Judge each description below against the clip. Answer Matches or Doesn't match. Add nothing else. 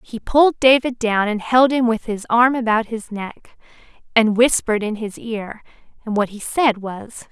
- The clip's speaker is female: Matches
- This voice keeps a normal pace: Matches